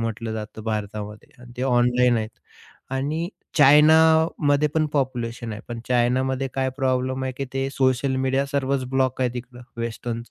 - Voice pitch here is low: Yes, low, 130 Hz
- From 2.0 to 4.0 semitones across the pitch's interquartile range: Yes, narrow, 2.4 semitones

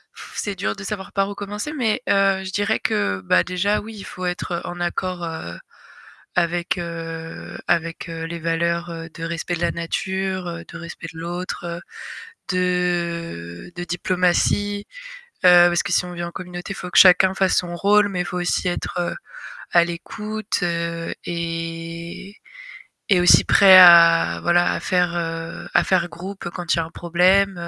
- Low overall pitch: No, medium, 175 Hz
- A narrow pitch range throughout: Yes, narrow, 2.0 semitones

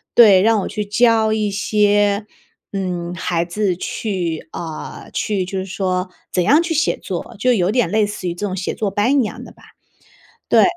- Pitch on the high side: Yes, high, 205 Hz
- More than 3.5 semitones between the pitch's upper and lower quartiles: No, average, 2.9 semitones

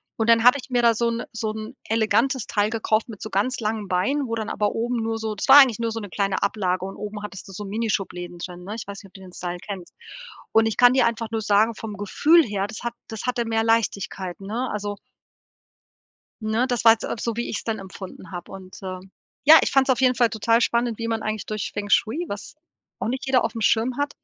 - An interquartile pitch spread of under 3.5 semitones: Yes, narrow, 2.6 semitones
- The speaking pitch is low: No, high, 220 Hz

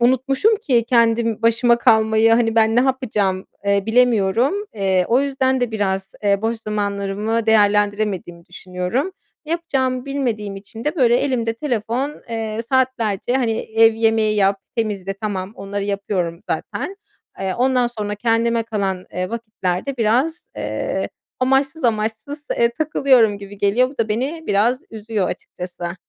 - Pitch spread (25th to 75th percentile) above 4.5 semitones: No, average, 3.8 semitones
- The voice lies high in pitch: Yes, high, 225 Hz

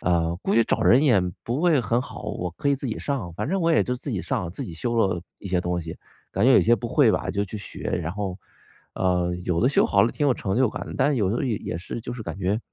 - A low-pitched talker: Yes, low, 105 Hz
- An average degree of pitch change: No, wide, 5.8 semitones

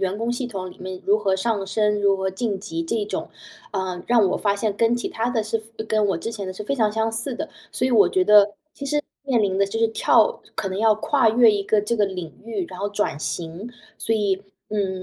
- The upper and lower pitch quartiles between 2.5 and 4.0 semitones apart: Yes, average, 2.9 semitones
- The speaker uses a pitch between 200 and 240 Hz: Yes, high, 210 Hz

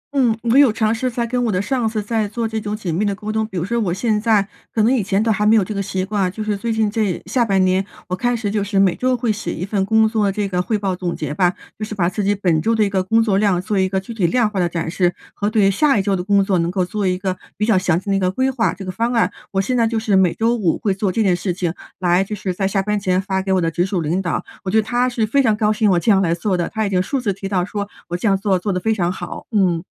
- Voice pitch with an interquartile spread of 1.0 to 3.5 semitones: Yes, average, 2.9 semitones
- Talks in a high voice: Yes, high, 200 Hz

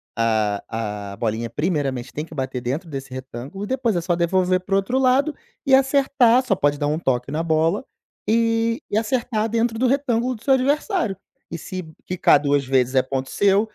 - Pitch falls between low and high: Yes, medium, 180 Hz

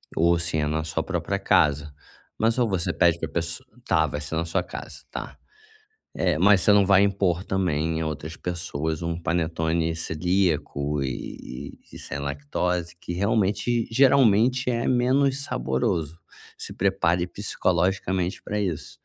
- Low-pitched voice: Yes, very low, 85 Hz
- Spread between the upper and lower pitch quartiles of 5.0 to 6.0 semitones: No, average, 3.8 semitones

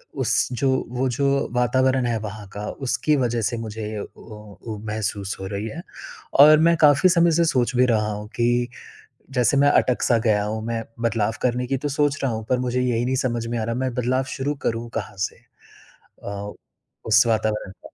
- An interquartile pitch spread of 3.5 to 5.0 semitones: No, average, 3.0 semitones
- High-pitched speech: No, low, 120 Hz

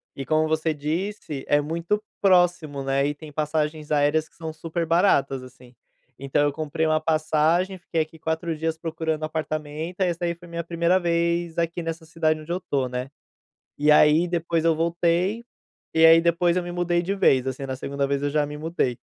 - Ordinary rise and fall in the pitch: No, narrow, 2.2 semitones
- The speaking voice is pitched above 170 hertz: No, medium, 160 Hz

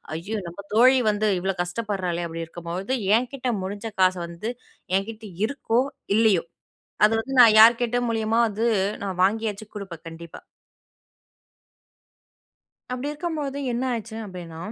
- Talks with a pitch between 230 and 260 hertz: No, high, 215 Hz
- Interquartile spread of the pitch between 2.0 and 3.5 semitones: No, average, 4.3 semitones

